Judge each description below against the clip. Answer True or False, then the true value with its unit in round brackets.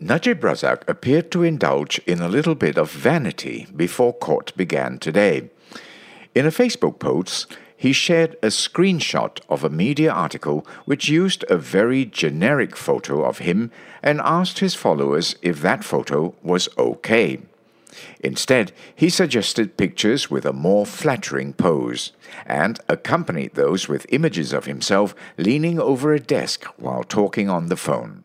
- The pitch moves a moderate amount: False (8.3 semitones)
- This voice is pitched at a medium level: True (145 Hz)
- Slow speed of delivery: False (145 wpm)